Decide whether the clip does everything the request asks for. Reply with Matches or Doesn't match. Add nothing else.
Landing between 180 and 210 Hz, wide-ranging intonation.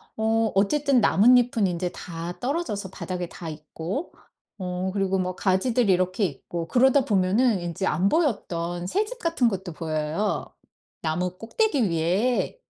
Matches